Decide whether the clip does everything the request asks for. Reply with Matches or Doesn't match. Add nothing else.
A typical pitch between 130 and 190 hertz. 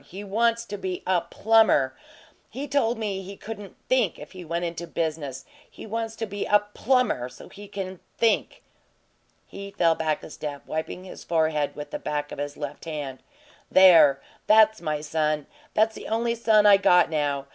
Matches